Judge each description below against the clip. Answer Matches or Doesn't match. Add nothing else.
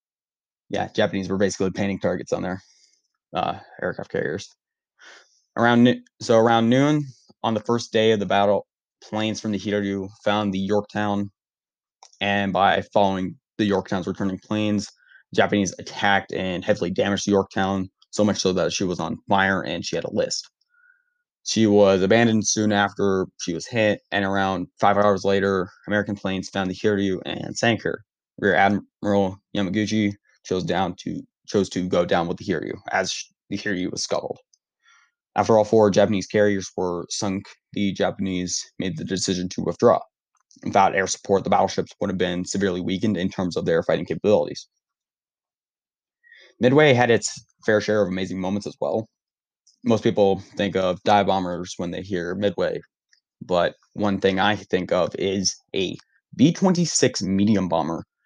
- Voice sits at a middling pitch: Doesn't match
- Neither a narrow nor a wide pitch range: Doesn't match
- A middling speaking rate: Matches